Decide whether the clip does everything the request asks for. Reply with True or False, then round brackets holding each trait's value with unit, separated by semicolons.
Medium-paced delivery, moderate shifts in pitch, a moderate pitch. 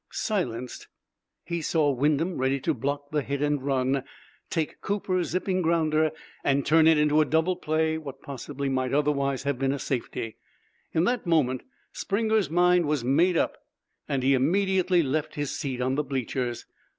True (165 wpm; 3.6 semitones; 150 Hz)